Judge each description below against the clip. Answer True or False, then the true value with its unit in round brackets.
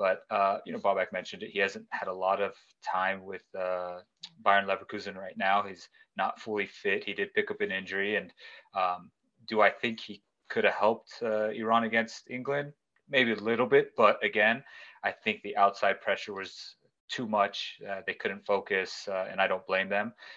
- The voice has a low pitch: True (110 Hz)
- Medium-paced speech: True (195 wpm)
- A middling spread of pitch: False (6.6 semitones)